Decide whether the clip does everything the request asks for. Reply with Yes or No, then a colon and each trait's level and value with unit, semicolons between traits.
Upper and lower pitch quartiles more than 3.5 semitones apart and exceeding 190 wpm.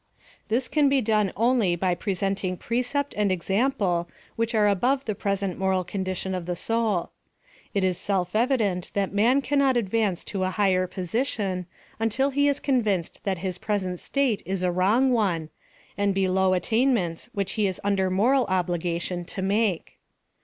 No: average, 3.9 semitones; average, 165 wpm